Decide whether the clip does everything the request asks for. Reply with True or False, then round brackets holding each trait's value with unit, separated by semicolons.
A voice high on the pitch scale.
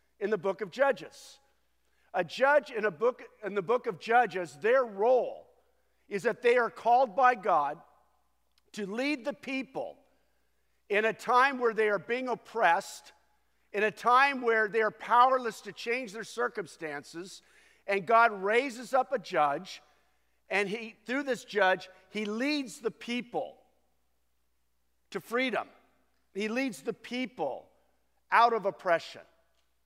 True (225 Hz)